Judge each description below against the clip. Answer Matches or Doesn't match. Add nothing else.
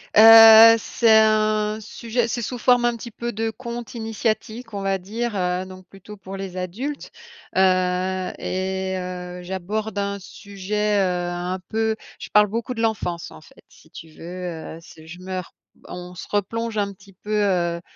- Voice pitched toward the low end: Doesn't match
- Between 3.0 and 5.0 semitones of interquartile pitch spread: Matches